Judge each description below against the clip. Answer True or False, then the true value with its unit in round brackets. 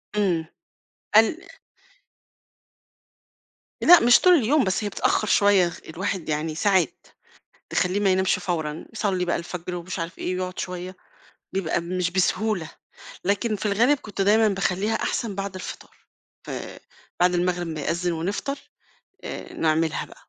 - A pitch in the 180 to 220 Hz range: True (185 Hz)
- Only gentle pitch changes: False (3.0 semitones)